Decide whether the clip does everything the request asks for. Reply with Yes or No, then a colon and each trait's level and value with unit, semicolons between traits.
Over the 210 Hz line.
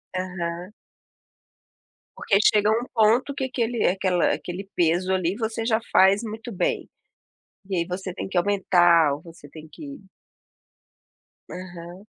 No: high, 190 Hz